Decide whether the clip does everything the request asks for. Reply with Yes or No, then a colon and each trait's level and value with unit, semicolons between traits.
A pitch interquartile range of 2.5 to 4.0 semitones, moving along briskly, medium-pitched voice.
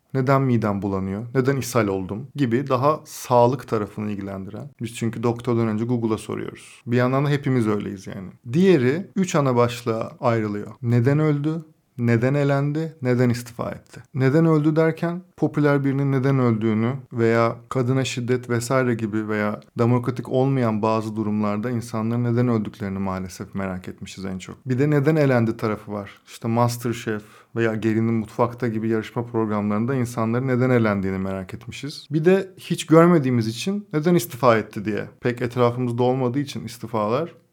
No: average, 3.6 semitones; fast, 150 wpm; low, 120 Hz